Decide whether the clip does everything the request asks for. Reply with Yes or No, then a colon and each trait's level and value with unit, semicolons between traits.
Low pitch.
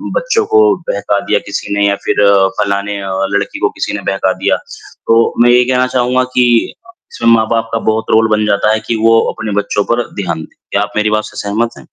Yes: low, 110 Hz